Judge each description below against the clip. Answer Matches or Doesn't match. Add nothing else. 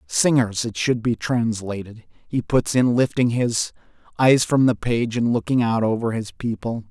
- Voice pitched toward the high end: Doesn't match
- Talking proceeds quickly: Doesn't match